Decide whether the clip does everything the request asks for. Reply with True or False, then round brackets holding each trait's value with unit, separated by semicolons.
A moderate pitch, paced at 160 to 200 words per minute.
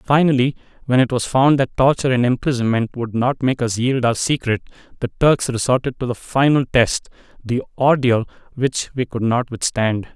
False (125 Hz; 170 wpm)